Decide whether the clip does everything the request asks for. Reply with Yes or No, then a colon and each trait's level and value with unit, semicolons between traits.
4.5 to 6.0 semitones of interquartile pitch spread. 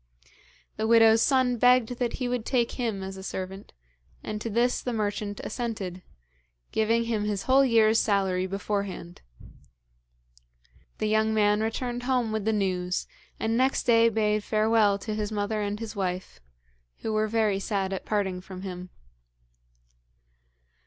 No: narrow, 2.5 semitones